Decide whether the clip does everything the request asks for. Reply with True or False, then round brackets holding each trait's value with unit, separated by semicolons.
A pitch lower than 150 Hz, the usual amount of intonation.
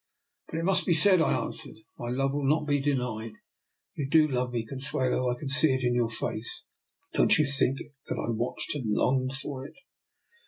True (135 Hz; 3.1 semitones)